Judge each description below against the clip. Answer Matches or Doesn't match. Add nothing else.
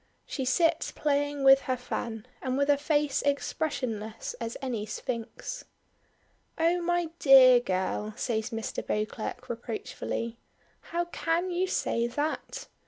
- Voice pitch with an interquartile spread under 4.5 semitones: Doesn't match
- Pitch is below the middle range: Doesn't match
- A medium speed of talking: Doesn't match